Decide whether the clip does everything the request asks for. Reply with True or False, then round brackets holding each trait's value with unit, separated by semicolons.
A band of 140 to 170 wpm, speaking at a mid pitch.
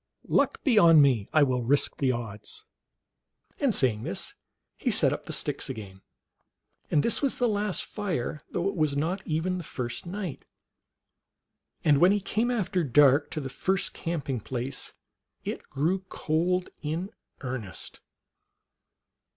True (150 wpm; 155 Hz)